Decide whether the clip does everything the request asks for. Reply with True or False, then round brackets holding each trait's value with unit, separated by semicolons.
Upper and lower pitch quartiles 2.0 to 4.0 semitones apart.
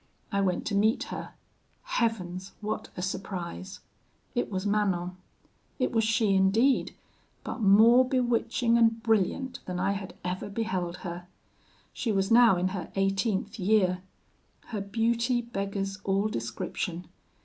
True (3.4 semitones)